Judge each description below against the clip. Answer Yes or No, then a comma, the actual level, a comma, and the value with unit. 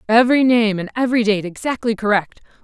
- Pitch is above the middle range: Yes, high, 225 Hz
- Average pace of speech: Yes, average, 160 wpm